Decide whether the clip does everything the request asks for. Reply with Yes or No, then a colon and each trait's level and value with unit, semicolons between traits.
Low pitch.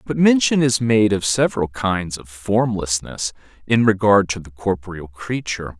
Yes: low, 100 Hz